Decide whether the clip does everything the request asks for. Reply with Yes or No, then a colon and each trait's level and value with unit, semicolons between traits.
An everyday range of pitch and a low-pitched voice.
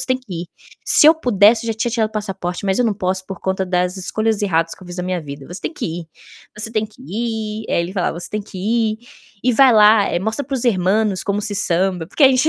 No: average, 3.4 semitones; high, 210 Hz